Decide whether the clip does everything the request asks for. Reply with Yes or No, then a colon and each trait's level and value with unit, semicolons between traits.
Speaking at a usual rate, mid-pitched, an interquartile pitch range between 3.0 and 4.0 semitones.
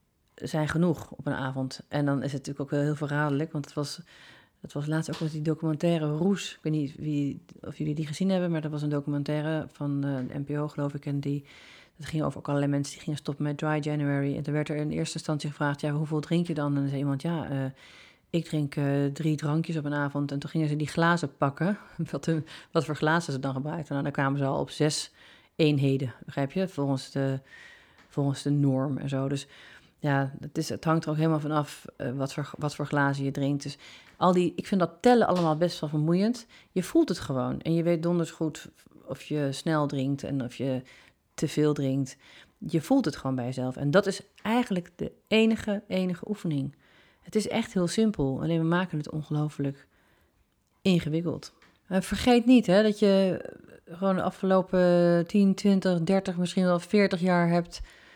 No: fast, 215 wpm; medium, 150 Hz; average, 3.6 semitones